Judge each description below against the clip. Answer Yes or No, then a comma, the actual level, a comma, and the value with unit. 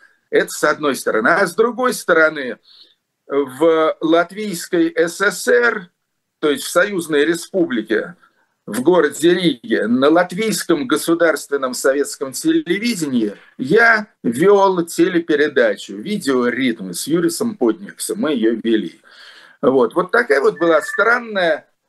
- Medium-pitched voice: Yes, medium, 175 Hz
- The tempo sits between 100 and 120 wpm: Yes, slow, 110 wpm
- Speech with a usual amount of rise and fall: No, wide, 5.8 semitones